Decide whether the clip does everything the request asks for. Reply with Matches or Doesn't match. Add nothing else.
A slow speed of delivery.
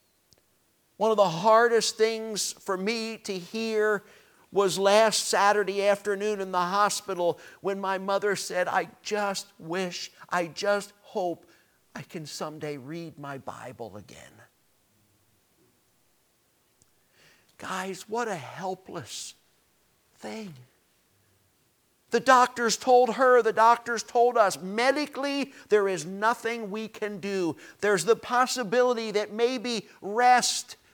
Matches